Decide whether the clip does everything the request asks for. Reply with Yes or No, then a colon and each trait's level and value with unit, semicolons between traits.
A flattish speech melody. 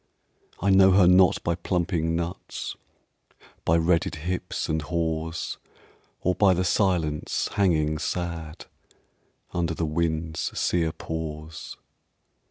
Yes: narrow, 2.2 semitones